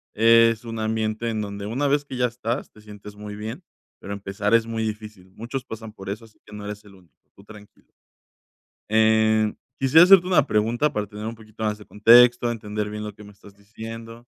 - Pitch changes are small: Yes, narrow, 1.8 semitones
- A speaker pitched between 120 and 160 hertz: No, low, 110 Hz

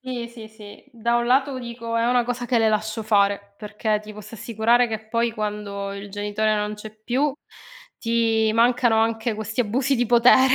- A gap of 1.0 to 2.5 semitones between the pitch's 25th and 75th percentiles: Yes, narrow, 2.1 semitones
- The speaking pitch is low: No, high, 225 Hz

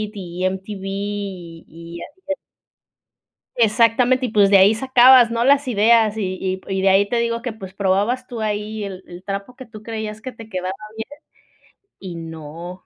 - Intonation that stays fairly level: No, average, 3.6 semitones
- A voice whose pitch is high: Yes, high, 205 Hz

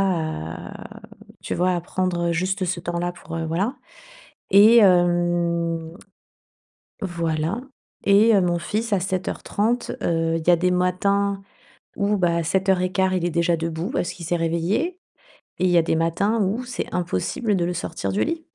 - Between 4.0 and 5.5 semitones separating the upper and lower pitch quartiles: No, average, 2.7 semitones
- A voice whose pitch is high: No, medium, 180 Hz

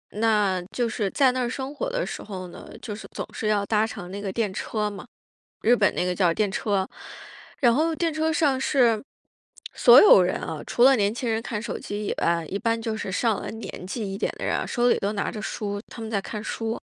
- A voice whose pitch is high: Yes, high, 220 Hz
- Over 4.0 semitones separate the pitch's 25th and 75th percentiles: No, average, 3.3 semitones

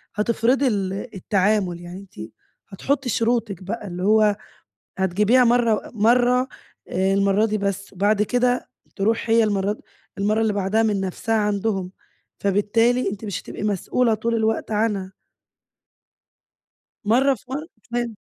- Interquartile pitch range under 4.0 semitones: Yes, average, 2.8 semitones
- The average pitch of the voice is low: No, high, 215 Hz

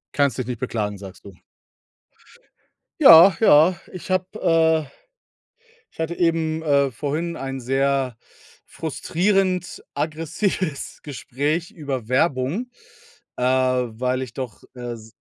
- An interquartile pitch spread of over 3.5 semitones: Yes, average, 4.5 semitones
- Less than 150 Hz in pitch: Yes, medium, 140 Hz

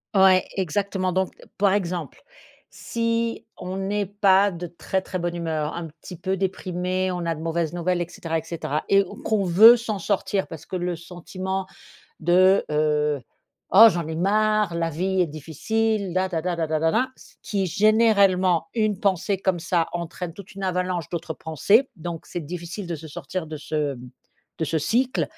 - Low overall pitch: No, medium, 180 Hz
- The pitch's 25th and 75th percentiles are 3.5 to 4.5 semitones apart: No, average, 3.0 semitones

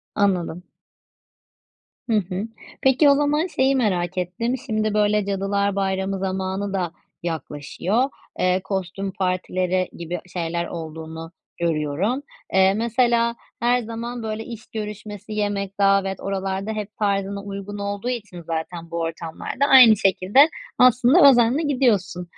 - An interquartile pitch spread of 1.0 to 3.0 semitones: No, average, 3.7 semitones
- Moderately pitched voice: No, high, 200 Hz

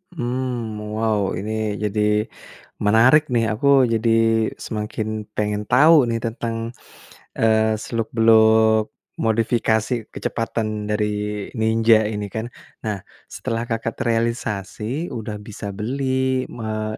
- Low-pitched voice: Yes, low, 110 Hz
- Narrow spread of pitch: Yes, narrow, 1.6 semitones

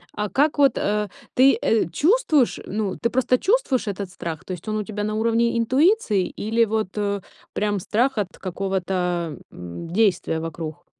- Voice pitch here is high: Yes, high, 210 Hz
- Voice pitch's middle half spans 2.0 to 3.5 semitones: No, average, 4.2 semitones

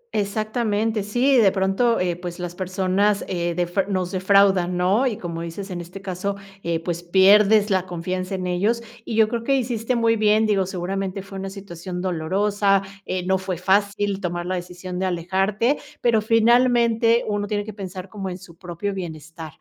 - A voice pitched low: No, high, 195 Hz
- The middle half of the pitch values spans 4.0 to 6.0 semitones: No, average, 2.8 semitones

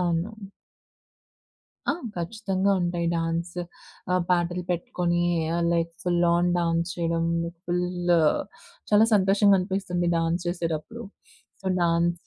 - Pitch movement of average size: No, narrow, 1.4 semitones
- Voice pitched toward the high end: No, medium, 175 Hz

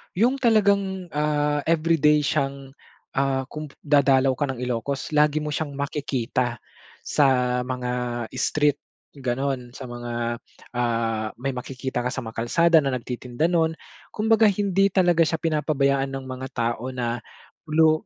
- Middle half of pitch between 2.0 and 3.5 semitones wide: No, average, 4.0 semitones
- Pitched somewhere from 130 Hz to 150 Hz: Yes, medium, 140 Hz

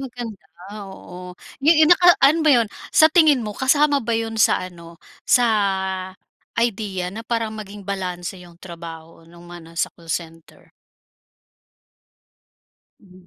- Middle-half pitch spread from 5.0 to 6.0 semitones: Yes, wide, 5.6 semitones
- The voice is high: Yes, high, 205 Hz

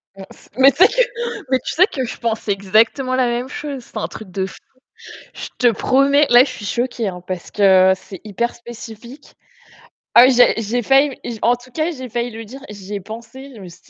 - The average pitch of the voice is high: Yes, high, 240 Hz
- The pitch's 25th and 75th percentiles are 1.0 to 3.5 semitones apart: No, average, 4.0 semitones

